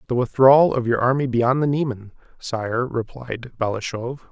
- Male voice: Yes, male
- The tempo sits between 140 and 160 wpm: Yes, average, 155 wpm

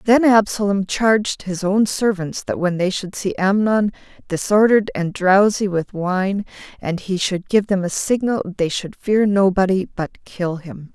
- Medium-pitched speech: No, high, 195 Hz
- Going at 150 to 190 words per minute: Yes, average, 170 wpm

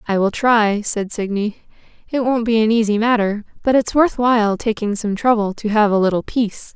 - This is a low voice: No, high, 220 Hz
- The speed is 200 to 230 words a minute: Yes, fast, 205 wpm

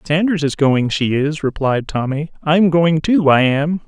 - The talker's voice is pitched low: No, medium, 150 Hz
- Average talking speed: Yes, average, 185 wpm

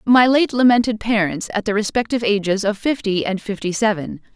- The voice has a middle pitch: No, high, 220 Hz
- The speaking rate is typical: Yes, average, 180 wpm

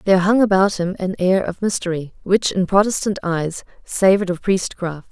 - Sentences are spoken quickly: No, average, 175 wpm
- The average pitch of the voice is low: No, high, 190 Hz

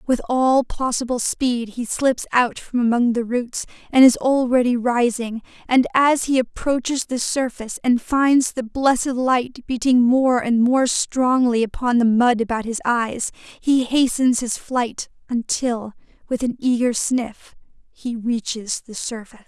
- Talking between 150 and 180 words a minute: Yes, average, 155 wpm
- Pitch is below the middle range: No, high, 245 Hz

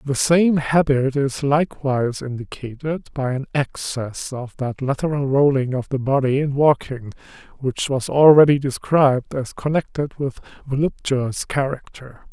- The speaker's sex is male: Yes, male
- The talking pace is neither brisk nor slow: No, slow, 130 wpm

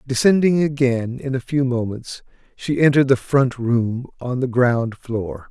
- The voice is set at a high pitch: No, low, 130 Hz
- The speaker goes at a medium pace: Yes, average, 165 wpm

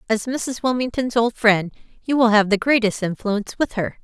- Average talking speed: Yes, average, 195 wpm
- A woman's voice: Yes, female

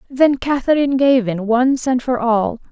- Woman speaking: Yes, female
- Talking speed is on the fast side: No, average, 175 wpm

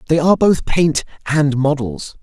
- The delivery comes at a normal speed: Yes, average, 160 wpm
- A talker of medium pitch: Yes, medium, 150 Hz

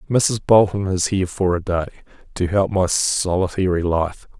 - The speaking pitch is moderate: No, very low, 95 Hz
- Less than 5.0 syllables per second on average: Yes, 4.8 syllables/s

